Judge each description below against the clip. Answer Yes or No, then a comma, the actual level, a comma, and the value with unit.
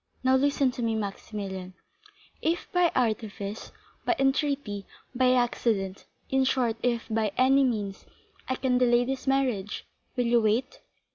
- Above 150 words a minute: No, slow, 135 wpm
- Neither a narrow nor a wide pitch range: Yes, average, 3.8 semitones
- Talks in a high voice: Yes, high, 245 Hz